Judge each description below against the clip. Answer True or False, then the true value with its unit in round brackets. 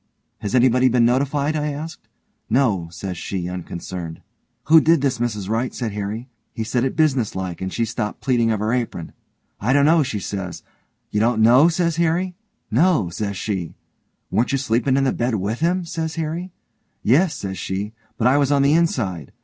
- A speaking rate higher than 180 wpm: True (190 wpm)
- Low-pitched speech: True (120 Hz)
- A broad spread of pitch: True (6.1 semitones)